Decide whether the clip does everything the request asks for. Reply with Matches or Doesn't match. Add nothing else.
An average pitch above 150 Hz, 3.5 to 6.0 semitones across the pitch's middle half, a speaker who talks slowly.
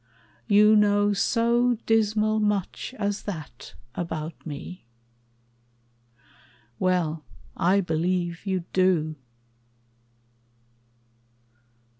Matches